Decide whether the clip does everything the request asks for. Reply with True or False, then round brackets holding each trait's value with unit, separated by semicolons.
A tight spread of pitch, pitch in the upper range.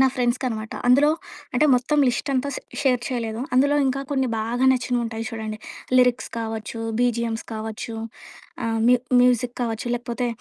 True (2.0 semitones; 245 Hz)